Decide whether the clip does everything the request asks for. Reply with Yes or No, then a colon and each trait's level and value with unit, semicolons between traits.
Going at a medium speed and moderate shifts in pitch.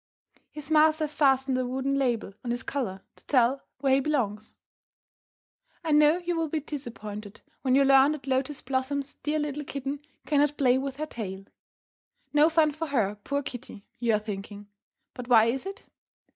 Yes: average, 175 wpm; average, 3.7 semitones